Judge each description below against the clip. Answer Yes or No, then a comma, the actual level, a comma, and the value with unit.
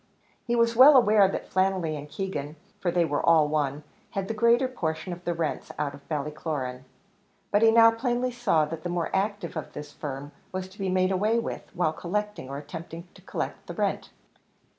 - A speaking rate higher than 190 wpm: Yes, average, 200 wpm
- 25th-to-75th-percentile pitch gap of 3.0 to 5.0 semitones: No, wide, 5.6 semitones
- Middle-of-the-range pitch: Yes, medium, 175 Hz